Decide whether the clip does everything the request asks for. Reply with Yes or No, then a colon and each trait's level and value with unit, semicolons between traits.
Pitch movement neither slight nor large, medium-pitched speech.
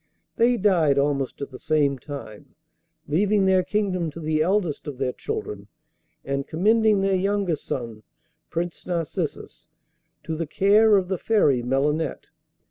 No: wide, 5.9 semitones; medium, 165 Hz